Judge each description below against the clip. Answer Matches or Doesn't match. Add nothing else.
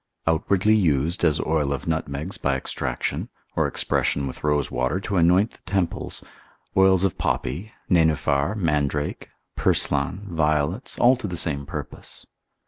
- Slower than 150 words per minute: Matches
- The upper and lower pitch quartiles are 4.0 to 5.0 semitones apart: Matches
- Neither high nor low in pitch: Doesn't match